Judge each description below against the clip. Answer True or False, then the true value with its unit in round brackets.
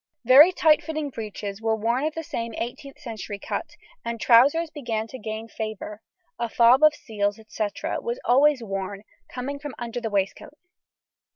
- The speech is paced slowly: False (165 wpm)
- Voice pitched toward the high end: True (235 Hz)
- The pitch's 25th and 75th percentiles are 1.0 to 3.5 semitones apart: False (4.8 semitones)